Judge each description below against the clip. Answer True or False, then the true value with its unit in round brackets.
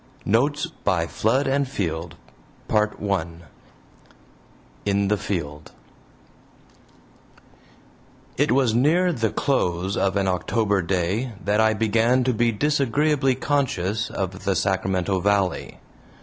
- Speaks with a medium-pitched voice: False (105 Hz)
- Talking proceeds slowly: True (110 wpm)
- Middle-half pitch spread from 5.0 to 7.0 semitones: True (5.5 semitones)